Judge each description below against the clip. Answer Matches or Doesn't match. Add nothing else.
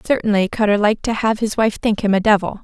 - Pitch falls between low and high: Doesn't match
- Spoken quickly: Matches